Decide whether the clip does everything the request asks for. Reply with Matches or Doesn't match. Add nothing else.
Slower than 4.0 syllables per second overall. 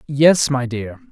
Matches